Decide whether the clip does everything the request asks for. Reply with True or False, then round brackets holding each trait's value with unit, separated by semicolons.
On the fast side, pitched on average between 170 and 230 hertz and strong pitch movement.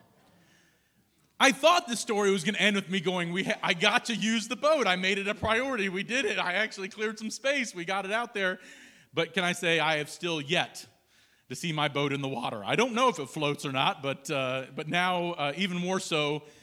True (245 wpm; 190 Hz; 5.8 semitones)